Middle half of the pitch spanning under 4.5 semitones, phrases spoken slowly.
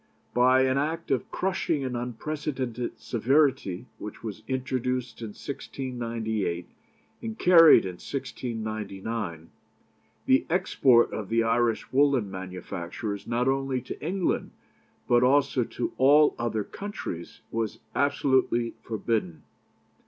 Yes: average, 3.8 semitones; slow, 110 wpm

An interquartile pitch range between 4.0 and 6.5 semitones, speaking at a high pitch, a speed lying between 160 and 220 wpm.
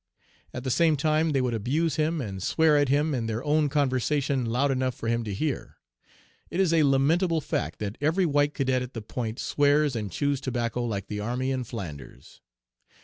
No: average, 4.3 semitones; low, 135 Hz; average, 200 wpm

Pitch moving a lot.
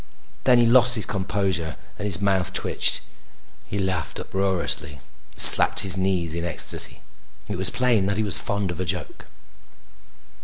No: narrow, 2.6 semitones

